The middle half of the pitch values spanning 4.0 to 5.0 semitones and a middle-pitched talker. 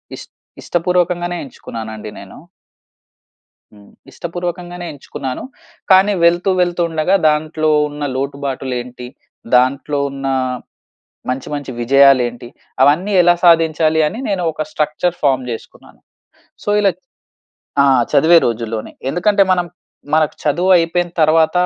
Yes: average, 4.5 semitones; medium, 155 Hz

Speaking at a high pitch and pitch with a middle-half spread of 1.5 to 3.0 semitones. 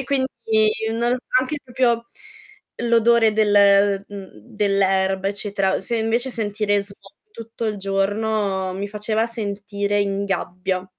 Yes: high, 205 Hz; narrow, 2.6 semitones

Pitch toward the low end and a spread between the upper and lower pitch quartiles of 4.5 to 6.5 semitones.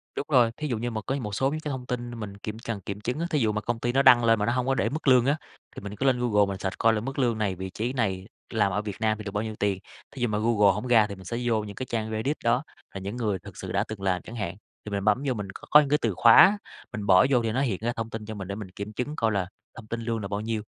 No: low, 110 Hz; average, 3.1 semitones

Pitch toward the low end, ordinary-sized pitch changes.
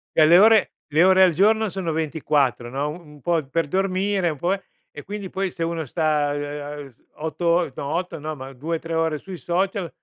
No: medium, 165 Hz; average, 3.8 semitones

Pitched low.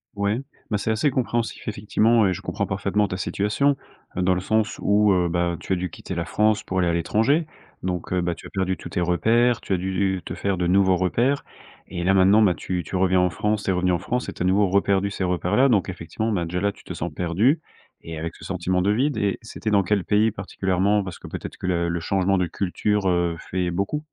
Yes: very low, 95 Hz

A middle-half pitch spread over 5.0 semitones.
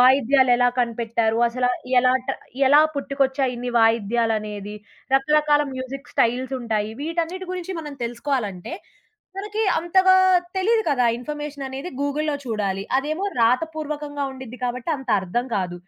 No: average, 4.3 semitones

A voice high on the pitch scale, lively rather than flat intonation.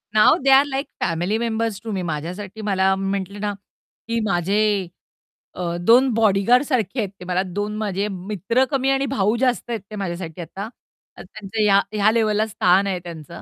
No: high, 205 Hz; average, 3.4 semitones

